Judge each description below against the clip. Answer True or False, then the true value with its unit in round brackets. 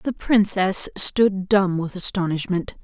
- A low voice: False (190 Hz)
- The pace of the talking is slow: True (125 wpm)